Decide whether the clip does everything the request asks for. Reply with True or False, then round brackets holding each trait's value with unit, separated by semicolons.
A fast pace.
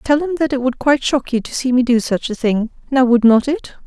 True (295 wpm)